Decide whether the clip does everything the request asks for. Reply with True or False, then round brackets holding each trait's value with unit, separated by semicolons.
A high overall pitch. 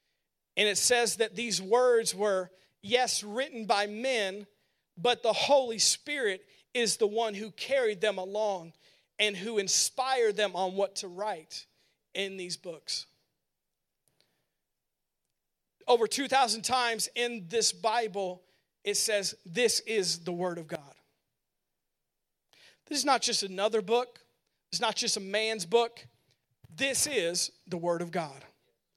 True (210 Hz)